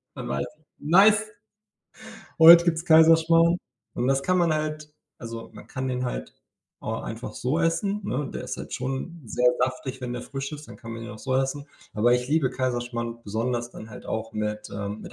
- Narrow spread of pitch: No, average, 5.3 semitones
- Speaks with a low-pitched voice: Yes, low, 130 Hz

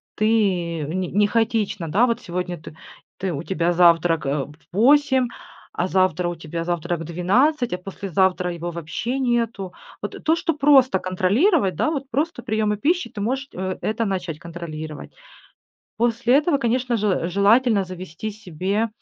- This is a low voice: No, high, 195 Hz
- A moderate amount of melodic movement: No, wide, 5.7 semitones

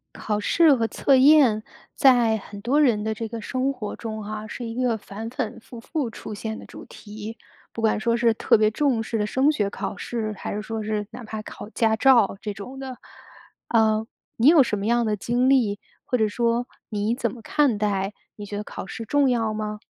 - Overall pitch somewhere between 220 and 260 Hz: Yes, high, 225 Hz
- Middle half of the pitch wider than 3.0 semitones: No, narrow, 2.6 semitones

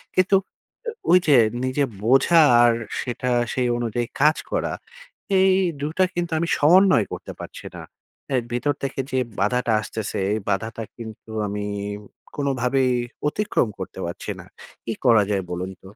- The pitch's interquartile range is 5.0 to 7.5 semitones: Yes, average, 5.3 semitones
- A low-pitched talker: Yes, low, 125 Hz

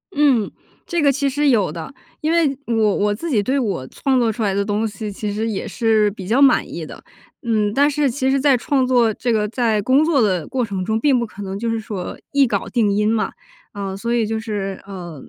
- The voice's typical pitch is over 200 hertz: Yes, high, 225 Hz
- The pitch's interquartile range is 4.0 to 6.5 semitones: Yes, average, 4.5 semitones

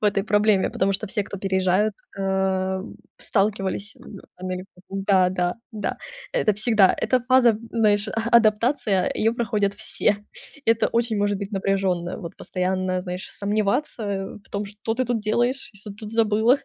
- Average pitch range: No, narrow, 2.3 semitones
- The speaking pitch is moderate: No, high, 205 Hz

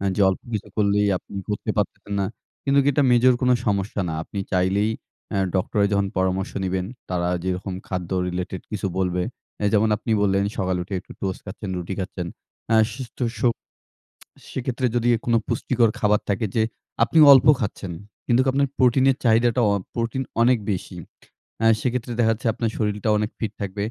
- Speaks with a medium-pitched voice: No, low, 105 Hz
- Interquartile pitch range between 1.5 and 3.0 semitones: No, average, 3.8 semitones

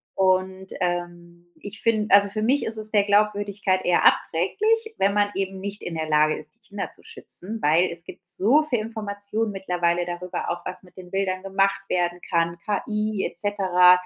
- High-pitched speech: Yes, high, 195 Hz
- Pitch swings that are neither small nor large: Yes, average, 3.0 semitones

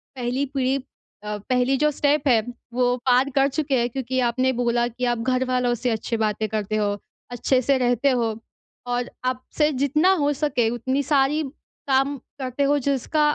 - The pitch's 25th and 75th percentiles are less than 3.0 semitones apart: Yes, narrow, 2.5 semitones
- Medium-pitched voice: No, very high, 255 Hz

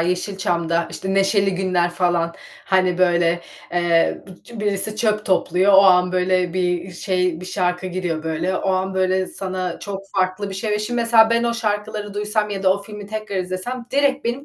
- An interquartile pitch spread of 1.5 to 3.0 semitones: Yes, narrow, 2.5 semitones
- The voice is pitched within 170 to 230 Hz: Yes, high, 190 Hz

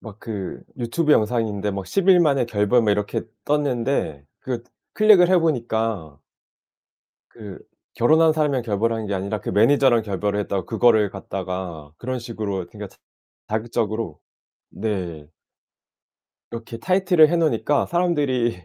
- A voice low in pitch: Yes, low, 115 Hz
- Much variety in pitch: Yes, wide, 5.8 semitones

